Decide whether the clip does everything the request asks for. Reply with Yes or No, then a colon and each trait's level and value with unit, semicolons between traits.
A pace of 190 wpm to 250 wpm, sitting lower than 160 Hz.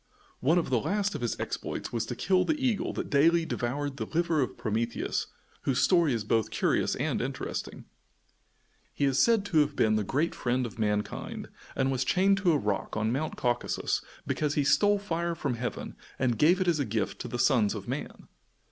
Yes: average, 200 wpm; medium, 140 Hz